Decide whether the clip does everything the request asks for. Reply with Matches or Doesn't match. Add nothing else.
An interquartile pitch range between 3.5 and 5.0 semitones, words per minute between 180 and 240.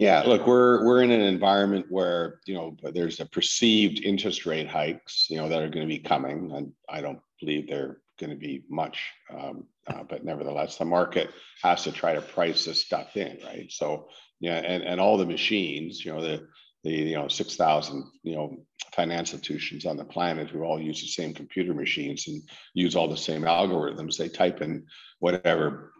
Matches